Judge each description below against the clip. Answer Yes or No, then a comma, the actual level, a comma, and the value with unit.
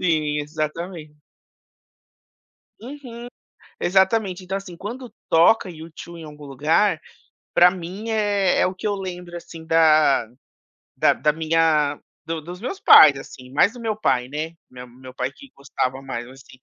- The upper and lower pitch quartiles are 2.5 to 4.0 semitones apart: No, average, 4.5 semitones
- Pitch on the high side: No, medium, 165 Hz